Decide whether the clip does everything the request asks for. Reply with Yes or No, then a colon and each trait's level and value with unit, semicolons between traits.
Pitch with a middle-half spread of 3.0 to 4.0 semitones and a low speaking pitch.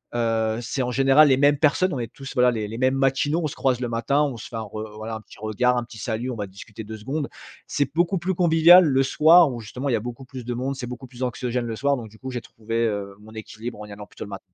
Yes: average, 3.7 semitones; low, 125 Hz